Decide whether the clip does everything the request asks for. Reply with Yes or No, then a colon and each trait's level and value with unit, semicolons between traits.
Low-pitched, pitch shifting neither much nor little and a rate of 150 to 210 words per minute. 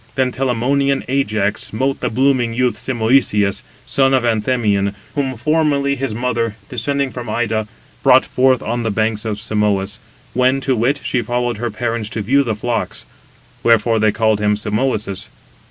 Yes: low, 120 Hz; average, 3.4 semitones; average, 155 wpm